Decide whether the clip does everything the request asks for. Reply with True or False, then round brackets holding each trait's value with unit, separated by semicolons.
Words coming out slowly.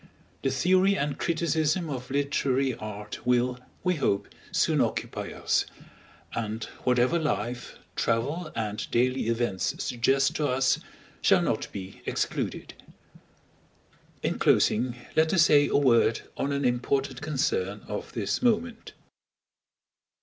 True (120 wpm)